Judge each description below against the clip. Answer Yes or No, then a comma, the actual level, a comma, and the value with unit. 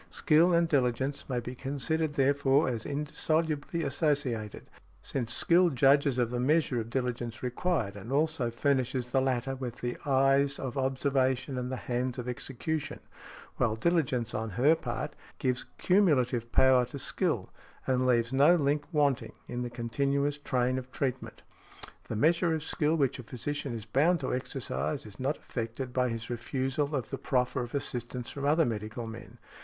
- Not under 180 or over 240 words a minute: No, average, 165 wpm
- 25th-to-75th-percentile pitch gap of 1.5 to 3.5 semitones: Yes, average, 3.0 semitones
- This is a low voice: Yes, low, 130 Hz